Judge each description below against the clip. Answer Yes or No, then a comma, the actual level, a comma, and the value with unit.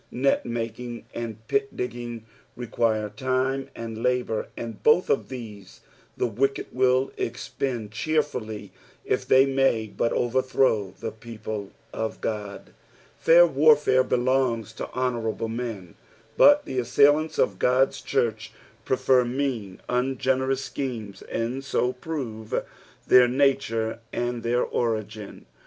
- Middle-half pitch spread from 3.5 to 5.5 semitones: No, average, 2.9 semitones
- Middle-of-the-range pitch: No, low, 120 Hz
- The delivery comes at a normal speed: No, slow, 120 wpm